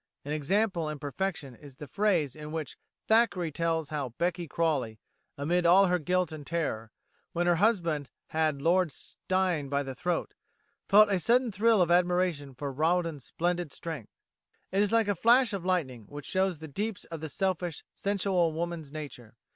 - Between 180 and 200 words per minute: No, average, 170 wpm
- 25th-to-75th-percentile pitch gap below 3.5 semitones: No, average, 4.1 semitones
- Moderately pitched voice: Yes, medium, 170 Hz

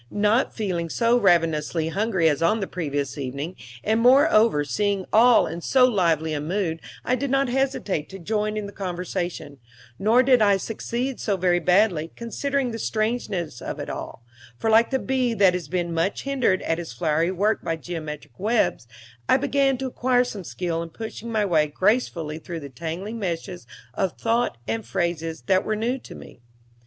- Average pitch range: No, wide, 5.8 semitones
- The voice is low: No, high, 190 Hz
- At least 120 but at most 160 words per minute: No, average, 185 wpm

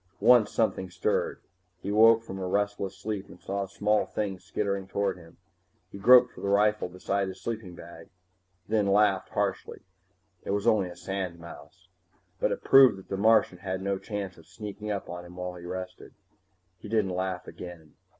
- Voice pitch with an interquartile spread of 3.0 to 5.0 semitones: No, narrow, 2.5 semitones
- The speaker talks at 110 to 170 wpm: No, average, 180 wpm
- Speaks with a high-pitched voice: No, low, 100 Hz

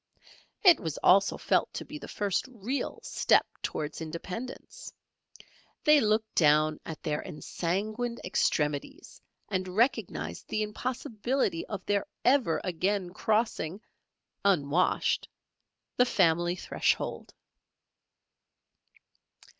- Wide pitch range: Yes, wide, 5.8 semitones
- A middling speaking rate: No, slow, 100 wpm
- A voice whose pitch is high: Yes, high, 195 Hz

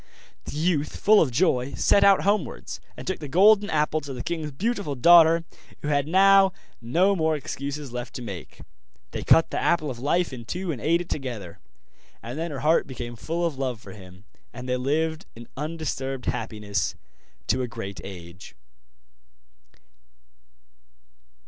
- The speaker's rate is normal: Yes, average, 165 wpm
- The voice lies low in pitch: No, medium, 145 Hz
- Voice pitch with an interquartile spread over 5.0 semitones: Yes, wide, 5.5 semitones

